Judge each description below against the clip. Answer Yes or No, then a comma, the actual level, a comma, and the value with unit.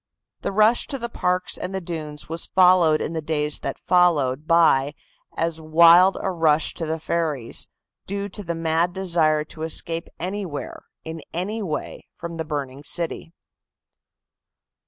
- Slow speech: No, average, 155 wpm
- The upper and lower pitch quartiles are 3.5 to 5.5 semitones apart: No, average, 2.7 semitones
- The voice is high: No, medium, 165 Hz